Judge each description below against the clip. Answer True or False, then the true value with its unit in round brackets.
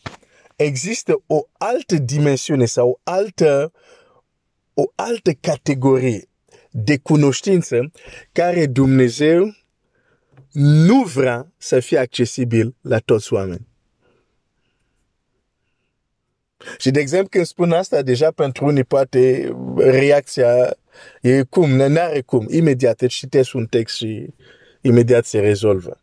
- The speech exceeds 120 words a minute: False (115 wpm)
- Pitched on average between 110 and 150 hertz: True (135 Hz)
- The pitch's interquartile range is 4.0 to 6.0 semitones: True (4.7 semitones)